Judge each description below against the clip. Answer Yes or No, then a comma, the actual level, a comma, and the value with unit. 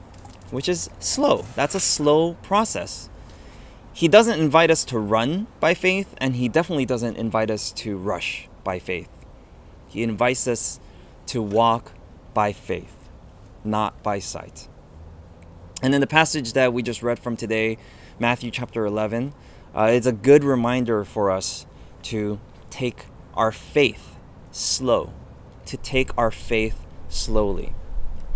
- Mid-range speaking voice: No, low, 115 Hz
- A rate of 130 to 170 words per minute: Yes, average, 140 wpm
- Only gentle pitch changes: No, average, 5.0 semitones